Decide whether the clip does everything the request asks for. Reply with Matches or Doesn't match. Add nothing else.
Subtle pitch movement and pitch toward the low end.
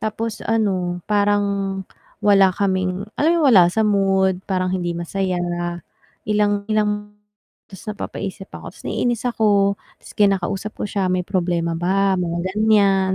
Doesn't match